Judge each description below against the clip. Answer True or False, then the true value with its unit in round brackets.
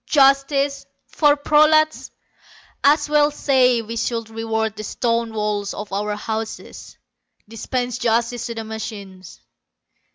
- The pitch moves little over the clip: False (3.9 semitones)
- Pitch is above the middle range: True (230 Hz)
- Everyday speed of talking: False (120 wpm)